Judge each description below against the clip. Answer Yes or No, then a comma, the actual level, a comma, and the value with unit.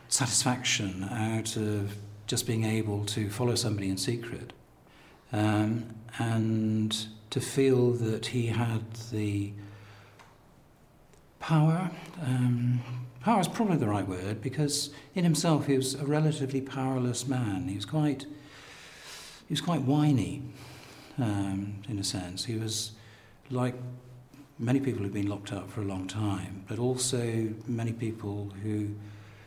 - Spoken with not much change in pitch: No, average, 4.2 semitones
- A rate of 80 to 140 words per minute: Yes, slow, 135 wpm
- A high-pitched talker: No, low, 115 Hz